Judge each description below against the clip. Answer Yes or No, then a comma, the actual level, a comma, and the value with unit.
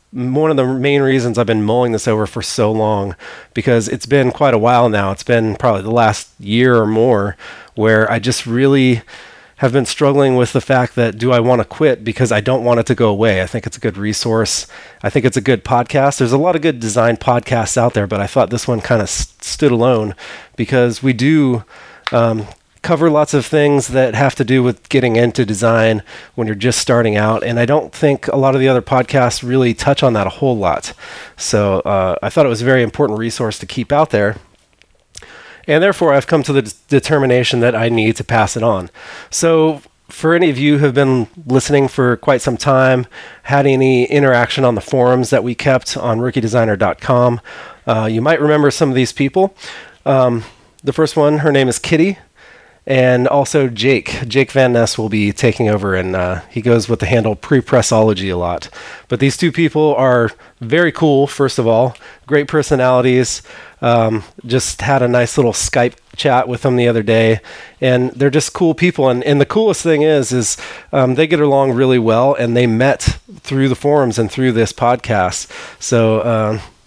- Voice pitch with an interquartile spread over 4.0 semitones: No, average, 3.4 semitones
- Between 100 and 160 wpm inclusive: No, fast, 205 wpm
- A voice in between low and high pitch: No, low, 125 Hz